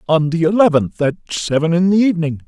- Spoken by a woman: No, male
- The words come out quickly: No, average, 195 wpm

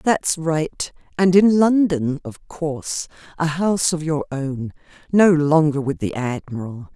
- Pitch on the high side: No, medium, 155 Hz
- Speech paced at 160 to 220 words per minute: No, average, 145 wpm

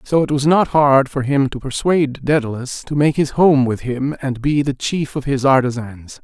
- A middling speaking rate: No, fast, 220 wpm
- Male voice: Yes, male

